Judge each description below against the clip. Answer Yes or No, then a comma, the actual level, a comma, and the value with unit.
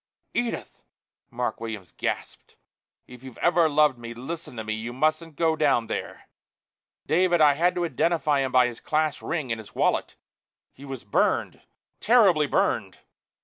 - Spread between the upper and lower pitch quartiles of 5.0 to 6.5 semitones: Yes, wide, 5.4 semitones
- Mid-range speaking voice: Yes, medium, 145 Hz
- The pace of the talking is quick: No, average, 155 wpm